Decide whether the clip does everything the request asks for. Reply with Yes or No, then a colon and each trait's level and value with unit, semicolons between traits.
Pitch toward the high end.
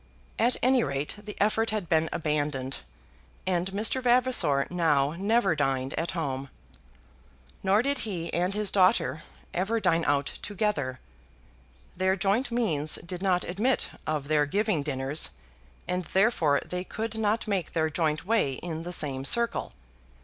No: medium, 180 Hz